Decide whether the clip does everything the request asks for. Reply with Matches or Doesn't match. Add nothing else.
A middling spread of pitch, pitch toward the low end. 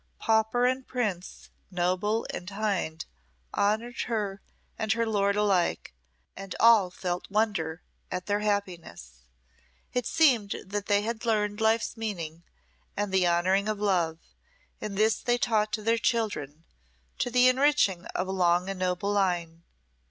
Doesn't match